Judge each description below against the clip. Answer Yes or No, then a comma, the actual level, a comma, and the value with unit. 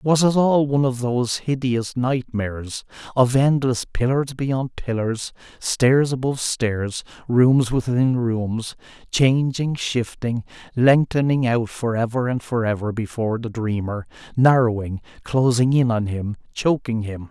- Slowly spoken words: Yes, slow, 130 wpm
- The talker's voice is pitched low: Yes, low, 120 Hz